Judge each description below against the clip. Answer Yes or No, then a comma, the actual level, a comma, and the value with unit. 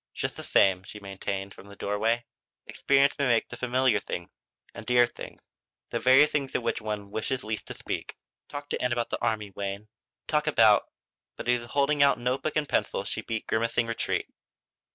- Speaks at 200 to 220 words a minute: Yes, fast, 205 wpm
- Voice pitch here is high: No, low, 115 Hz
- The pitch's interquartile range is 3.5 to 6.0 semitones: Yes, average, 4.0 semitones